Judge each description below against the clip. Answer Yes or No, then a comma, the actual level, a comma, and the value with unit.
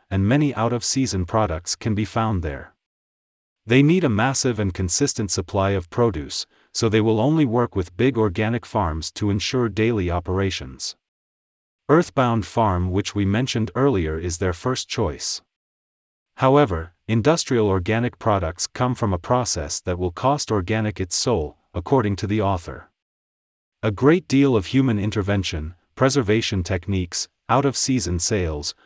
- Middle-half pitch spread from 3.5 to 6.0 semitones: Yes, average, 5.3 semitones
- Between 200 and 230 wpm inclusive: No, average, 150 wpm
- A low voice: Yes, low, 105 Hz